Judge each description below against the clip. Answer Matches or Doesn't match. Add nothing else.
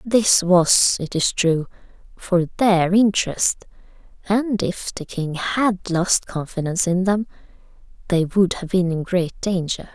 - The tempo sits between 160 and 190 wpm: Doesn't match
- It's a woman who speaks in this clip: Matches